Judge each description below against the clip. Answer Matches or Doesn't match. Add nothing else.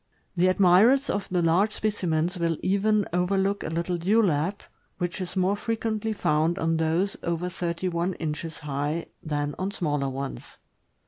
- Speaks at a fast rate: Doesn't match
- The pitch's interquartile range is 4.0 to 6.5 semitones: Doesn't match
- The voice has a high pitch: Doesn't match